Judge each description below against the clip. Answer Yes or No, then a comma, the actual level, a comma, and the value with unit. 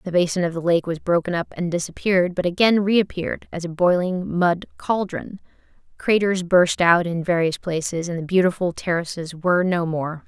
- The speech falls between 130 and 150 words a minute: No, average, 180 wpm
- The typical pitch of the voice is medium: Yes, medium, 175 Hz